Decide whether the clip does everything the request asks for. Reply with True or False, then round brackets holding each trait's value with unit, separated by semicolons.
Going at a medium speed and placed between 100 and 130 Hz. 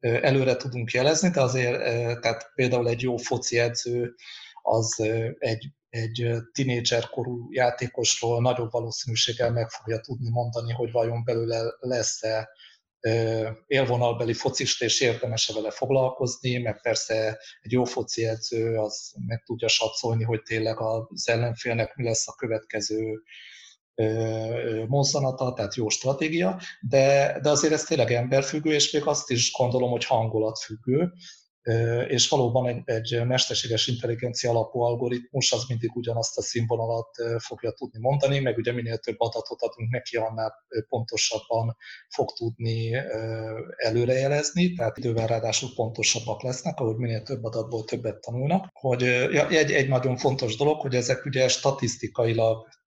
True (130 wpm; 120 Hz)